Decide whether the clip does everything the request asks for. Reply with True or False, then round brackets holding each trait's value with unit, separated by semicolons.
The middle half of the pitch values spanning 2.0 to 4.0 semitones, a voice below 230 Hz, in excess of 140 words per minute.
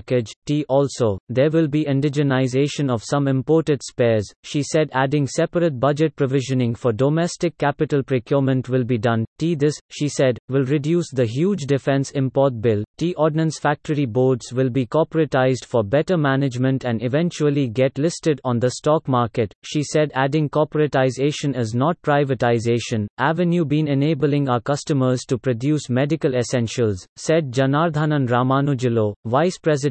True (3.2 semitones; 140 Hz; 150 wpm)